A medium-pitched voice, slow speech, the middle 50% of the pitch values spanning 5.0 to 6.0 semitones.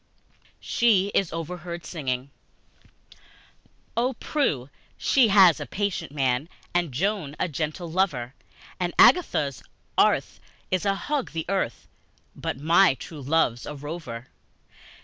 Yes: medium, 165 Hz; slow, 120 wpm; wide, 5.6 semitones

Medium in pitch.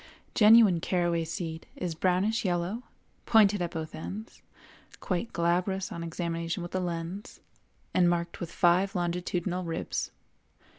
Yes: medium, 175 Hz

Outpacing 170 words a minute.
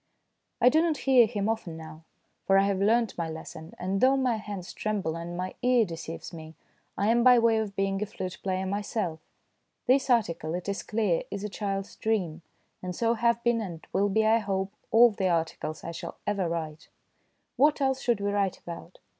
Yes: average, 200 wpm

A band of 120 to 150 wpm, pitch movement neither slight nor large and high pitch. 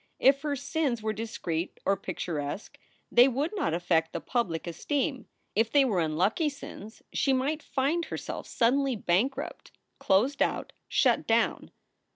No: average, 145 wpm; wide, 6.9 semitones; high, 240 Hz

